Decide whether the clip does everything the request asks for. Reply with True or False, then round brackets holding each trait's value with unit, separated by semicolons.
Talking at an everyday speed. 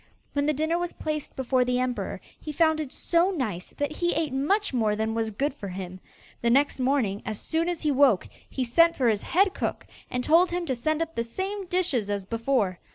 False (220 wpm)